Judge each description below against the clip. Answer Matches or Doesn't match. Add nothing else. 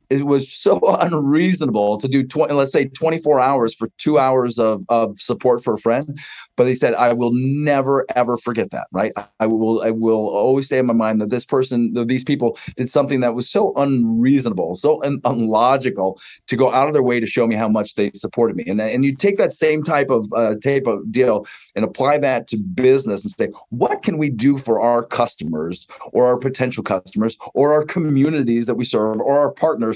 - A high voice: Doesn't match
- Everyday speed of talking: Doesn't match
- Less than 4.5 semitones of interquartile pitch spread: Matches